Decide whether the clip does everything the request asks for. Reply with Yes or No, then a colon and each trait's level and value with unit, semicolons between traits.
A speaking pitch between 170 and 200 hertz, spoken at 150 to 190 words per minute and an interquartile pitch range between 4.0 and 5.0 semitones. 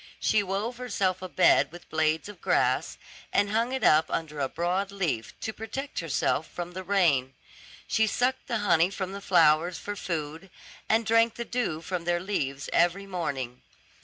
Yes: medium, 185 Hz; average, 175 wpm; average, 4.4 semitones